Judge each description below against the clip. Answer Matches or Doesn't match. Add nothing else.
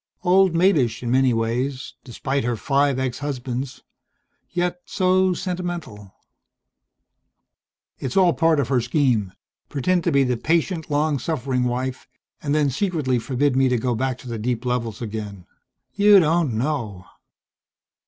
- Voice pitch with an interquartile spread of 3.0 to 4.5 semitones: Doesn't match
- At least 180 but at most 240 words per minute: Doesn't match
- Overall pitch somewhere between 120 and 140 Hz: Matches